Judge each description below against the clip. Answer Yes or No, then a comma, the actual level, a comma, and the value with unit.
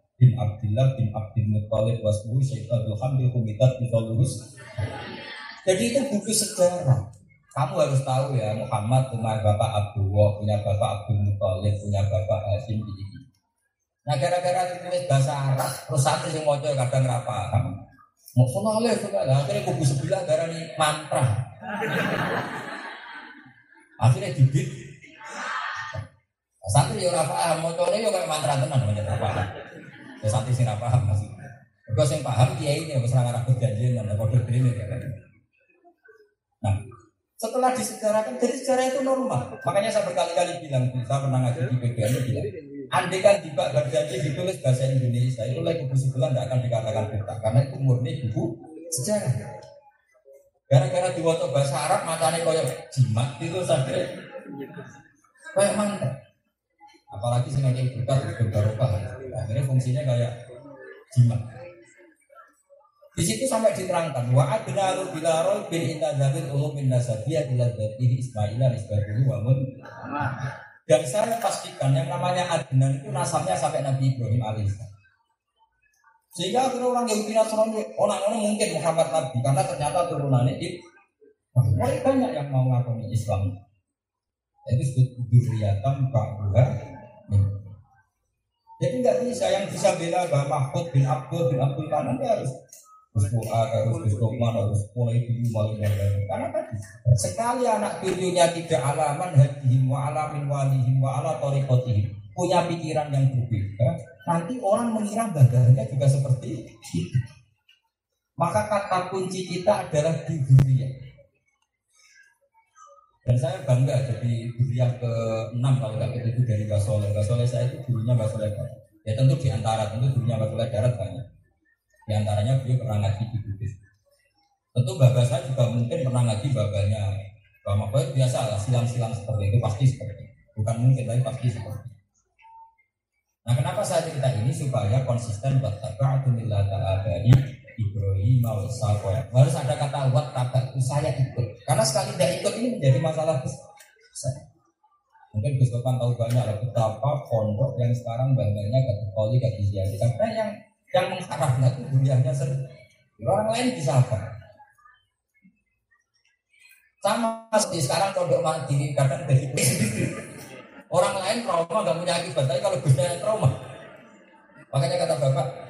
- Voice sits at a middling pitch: No, low, 130 Hz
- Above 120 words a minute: Yes, fast, 140 wpm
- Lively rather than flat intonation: Yes, wide, 5.7 semitones